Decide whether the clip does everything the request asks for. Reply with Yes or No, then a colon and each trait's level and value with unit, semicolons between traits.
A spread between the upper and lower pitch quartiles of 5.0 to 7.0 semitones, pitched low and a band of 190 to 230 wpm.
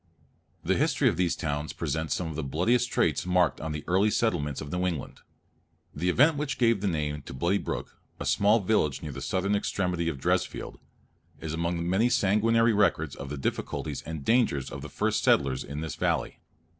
Yes: average, 5.3 semitones; very low, 85 Hz; average, 195 wpm